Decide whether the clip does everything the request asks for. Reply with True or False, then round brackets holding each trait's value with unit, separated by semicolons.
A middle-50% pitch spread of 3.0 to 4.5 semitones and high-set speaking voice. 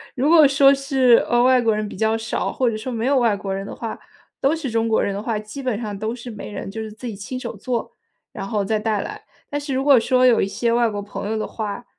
True (3.3 semitones; 230 Hz)